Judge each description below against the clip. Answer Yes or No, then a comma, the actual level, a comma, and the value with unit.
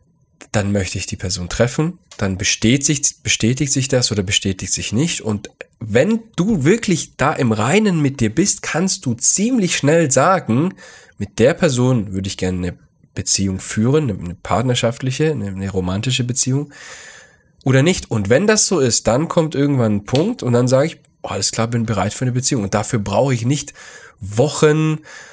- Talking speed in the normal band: Yes, average, 175 wpm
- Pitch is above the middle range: No, low, 125 Hz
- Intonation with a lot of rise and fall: Yes, wide, 7.1 semitones